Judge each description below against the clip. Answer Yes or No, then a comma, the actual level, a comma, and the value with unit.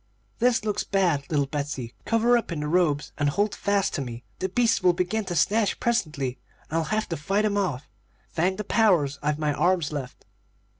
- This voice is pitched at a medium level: Yes, medium, 175 Hz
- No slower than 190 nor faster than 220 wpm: Yes, average, 200 wpm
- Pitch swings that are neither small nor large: No, wide, 5.8 semitones